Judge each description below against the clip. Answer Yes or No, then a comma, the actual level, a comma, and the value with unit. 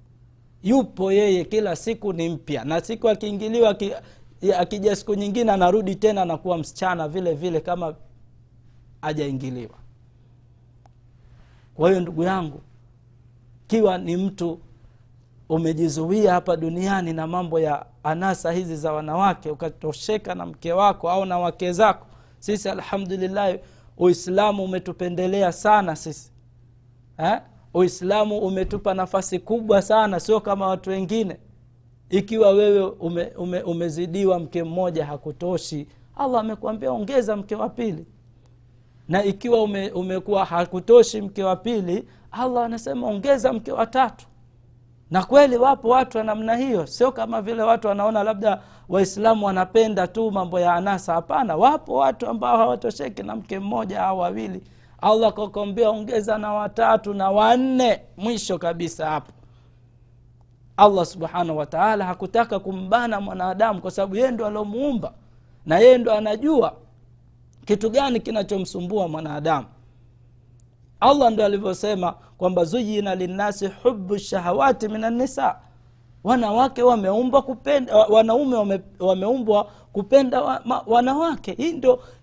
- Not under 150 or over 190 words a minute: No, average, 120 wpm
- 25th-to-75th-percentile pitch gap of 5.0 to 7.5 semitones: Yes, wide, 5.6 semitones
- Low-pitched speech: No, high, 190 Hz